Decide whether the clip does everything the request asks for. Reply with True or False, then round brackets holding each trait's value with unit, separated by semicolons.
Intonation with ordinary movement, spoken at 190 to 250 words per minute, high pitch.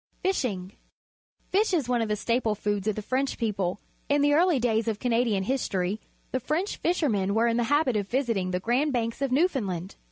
True (5.0 semitones; 200 wpm; 235 Hz)